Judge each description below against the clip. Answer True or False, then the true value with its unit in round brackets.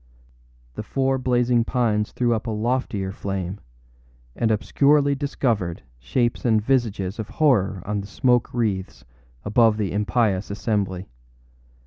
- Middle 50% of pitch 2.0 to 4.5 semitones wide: True (3.7 semitones)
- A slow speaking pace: True (125 wpm)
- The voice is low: True (110 Hz)